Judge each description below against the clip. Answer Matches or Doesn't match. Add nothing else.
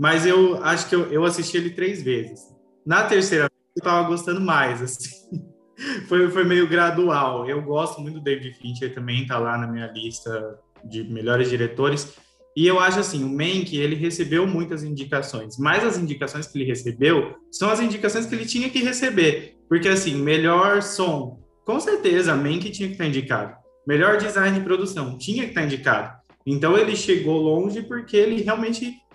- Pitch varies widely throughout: Matches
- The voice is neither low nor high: Matches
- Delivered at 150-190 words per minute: Matches